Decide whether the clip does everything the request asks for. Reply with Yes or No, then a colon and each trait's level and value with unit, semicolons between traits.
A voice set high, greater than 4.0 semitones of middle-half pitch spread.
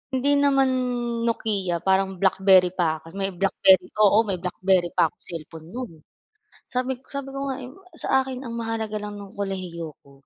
Yes: high, 195 Hz; average, 4.9 semitones